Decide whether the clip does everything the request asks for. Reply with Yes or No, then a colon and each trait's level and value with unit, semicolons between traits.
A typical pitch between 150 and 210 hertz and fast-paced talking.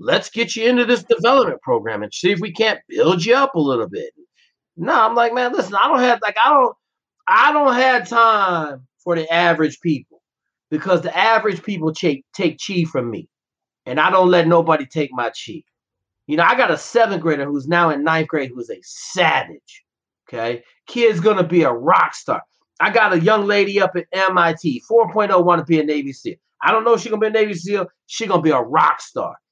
Yes: high, 190 Hz; fast, 220 wpm